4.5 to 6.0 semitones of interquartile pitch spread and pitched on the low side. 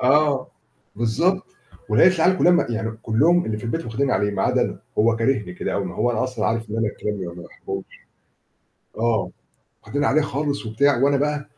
Yes: average, 4.8 semitones; low, 120 Hz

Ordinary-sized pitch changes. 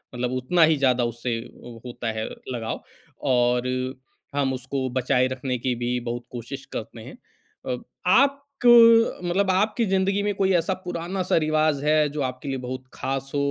No: wide, 6.4 semitones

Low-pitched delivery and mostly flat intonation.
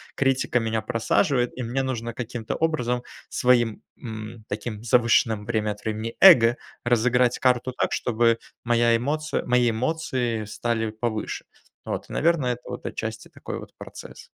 Yes: low, 120 Hz; narrow, 2.0 semitones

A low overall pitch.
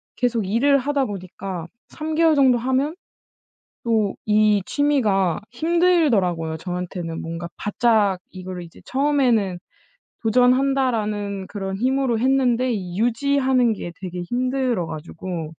No: high, 225 Hz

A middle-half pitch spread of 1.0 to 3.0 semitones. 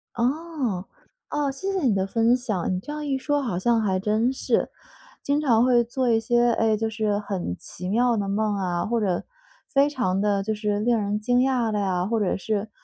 No: average, 3.7 semitones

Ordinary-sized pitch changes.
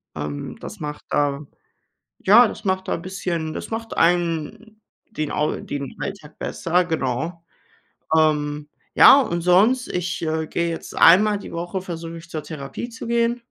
Yes: average, 4.3 semitones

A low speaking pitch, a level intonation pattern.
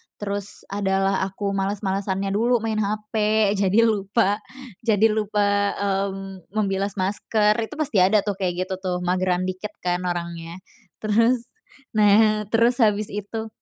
No: high, 200 Hz; narrow, 1.8 semitones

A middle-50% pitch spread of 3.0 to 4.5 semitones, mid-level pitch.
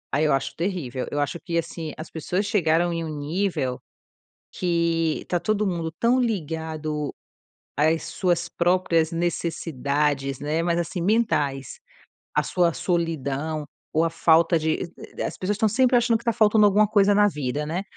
Yes: average, 3.6 semitones; medium, 165 Hz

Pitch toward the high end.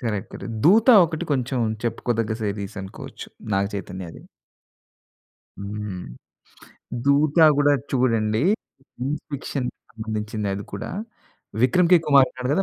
No: low, 120 Hz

